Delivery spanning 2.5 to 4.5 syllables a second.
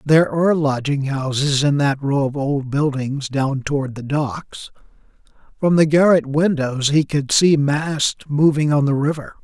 Yes: 4.4 syllables/s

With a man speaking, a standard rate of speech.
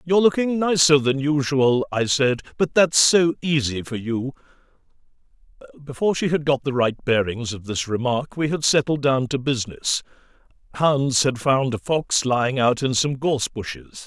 Yes: male; average, 170 wpm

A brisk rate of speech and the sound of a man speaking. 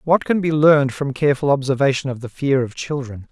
Yes: fast, 215 wpm; male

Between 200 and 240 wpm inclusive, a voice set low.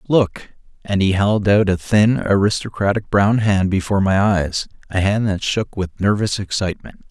No: average, 170 wpm; low, 100 Hz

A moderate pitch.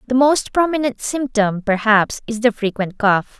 No: high, 230 Hz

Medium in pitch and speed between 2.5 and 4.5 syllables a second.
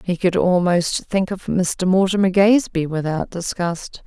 Yes: medium, 180 Hz; 4.3 syllables/s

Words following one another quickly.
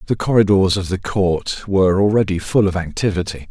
No: average, 170 wpm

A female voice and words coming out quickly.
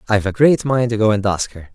No: male; fast, 310 wpm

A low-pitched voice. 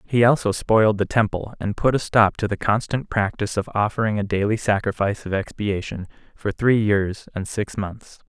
Yes: low, 105 Hz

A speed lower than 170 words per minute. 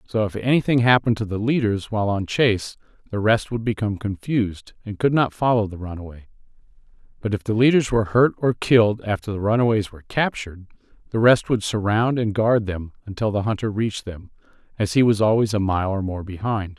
No: average, 195 wpm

